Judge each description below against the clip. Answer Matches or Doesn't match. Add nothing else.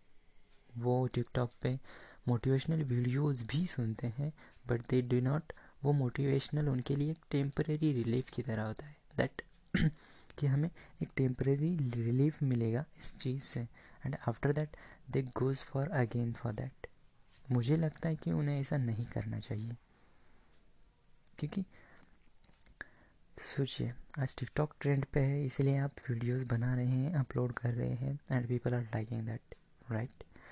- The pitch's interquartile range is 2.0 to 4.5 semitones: Matches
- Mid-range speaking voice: Doesn't match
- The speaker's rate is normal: Matches